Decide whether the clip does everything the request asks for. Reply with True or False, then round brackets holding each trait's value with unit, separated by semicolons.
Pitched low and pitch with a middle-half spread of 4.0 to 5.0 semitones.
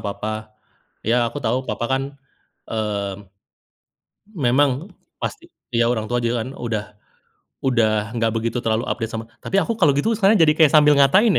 True (120 Hz; 4.6 semitones)